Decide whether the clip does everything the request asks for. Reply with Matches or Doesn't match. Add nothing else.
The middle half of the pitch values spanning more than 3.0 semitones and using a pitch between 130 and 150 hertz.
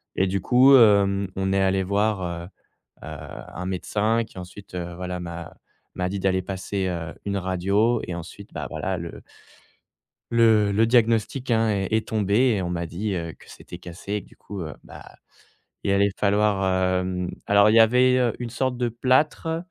Doesn't match